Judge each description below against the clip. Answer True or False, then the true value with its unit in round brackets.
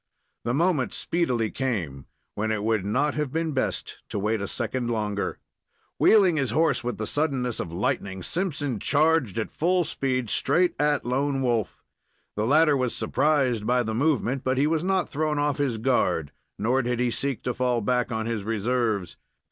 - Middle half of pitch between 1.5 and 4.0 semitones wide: False (4.8 semitones)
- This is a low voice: True (125 Hz)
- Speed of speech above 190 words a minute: False (180 wpm)